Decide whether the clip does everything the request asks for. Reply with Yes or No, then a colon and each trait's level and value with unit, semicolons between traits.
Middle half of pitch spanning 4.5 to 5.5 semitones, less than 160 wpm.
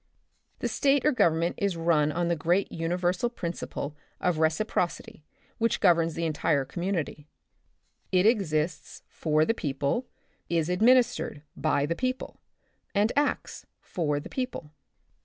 Yes: average, 5.2 semitones; slow, 135 wpm